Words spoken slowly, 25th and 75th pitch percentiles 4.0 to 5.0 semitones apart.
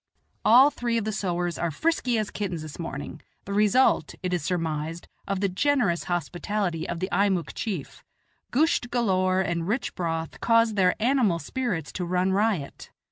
No: average, 165 wpm; average, 4.6 semitones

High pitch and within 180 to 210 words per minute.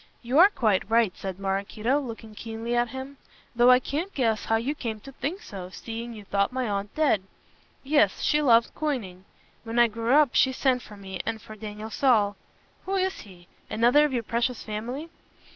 Yes: high, 235 Hz; average, 195 wpm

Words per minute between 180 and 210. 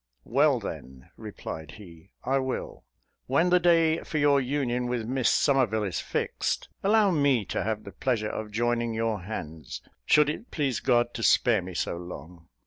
No: average, 170 wpm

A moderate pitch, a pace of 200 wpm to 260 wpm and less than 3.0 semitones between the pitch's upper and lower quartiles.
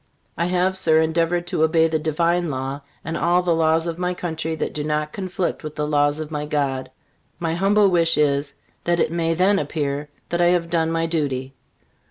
Yes: medium, 160 Hz; fast, 205 wpm; narrow, 2.4 semitones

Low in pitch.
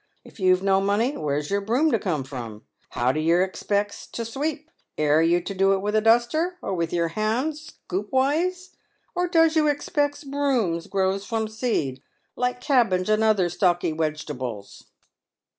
No: high, 205 Hz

